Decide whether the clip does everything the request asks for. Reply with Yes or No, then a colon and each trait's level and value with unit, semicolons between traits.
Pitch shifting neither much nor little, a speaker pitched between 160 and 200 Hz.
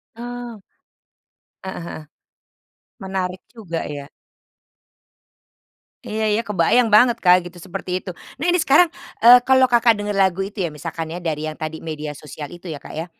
No: wide, 5.9 semitones; high, 190 Hz